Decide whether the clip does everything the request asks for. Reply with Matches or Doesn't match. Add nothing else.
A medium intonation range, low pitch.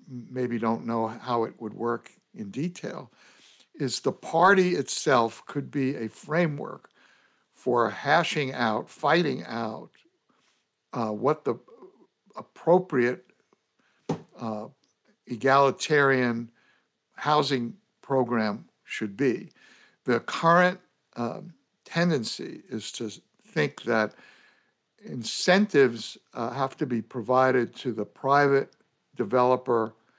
Doesn't match